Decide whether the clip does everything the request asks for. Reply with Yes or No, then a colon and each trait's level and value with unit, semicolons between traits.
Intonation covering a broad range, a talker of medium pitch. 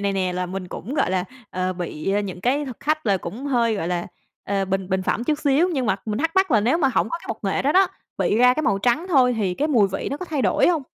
No: wide, 7.1 semitones; high, 230 Hz